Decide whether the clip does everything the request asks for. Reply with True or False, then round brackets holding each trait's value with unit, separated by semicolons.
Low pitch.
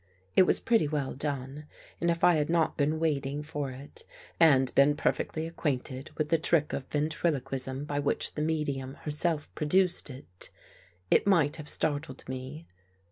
False (150 Hz)